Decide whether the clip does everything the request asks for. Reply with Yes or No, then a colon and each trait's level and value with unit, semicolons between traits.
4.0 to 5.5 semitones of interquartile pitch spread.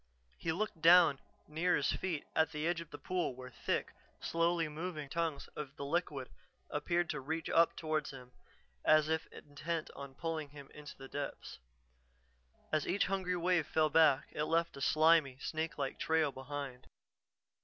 No: average, 2.8 semitones